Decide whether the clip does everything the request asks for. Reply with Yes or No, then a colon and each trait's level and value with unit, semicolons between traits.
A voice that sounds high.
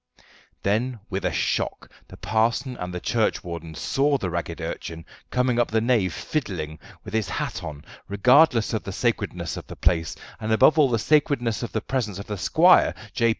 No: low, 110 Hz